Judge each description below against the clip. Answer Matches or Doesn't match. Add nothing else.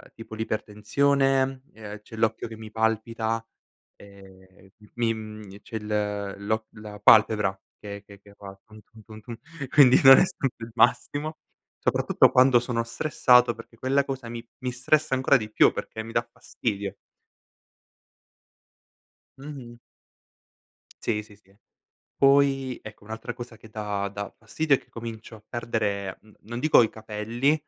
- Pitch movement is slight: Doesn't match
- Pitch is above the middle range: Doesn't match